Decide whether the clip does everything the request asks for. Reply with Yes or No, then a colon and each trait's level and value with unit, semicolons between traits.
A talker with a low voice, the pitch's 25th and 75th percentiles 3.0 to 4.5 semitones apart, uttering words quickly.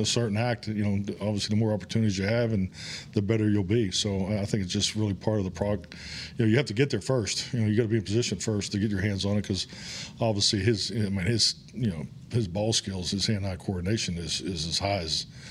No: low, 105 Hz; narrow, 2.4 semitones; fast, 265 wpm